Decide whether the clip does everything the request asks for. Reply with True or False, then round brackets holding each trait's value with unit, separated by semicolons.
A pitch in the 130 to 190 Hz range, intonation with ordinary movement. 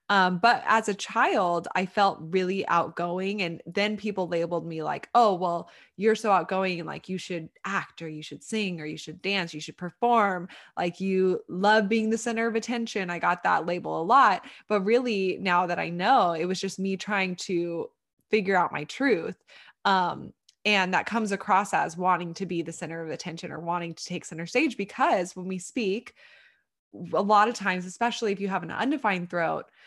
True (185 Hz; 3.2 semitones)